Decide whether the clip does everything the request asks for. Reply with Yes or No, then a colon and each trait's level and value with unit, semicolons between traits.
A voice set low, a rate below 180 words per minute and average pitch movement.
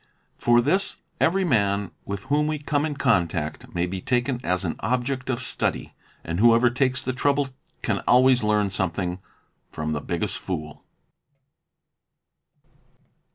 No: low, 120 Hz; average, 145 wpm; wide, 6.0 semitones